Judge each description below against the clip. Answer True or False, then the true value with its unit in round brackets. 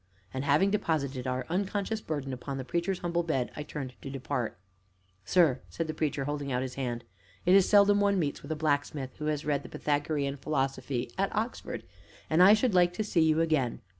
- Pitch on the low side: False (150 Hz)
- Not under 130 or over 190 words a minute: False (200 wpm)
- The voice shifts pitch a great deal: False (4.5 semitones)